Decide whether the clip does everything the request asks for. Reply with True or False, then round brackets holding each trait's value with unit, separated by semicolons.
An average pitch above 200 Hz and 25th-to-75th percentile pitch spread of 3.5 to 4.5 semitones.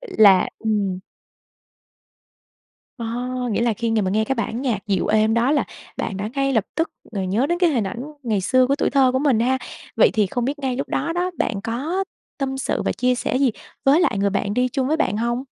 True (245 Hz; 4.1 semitones)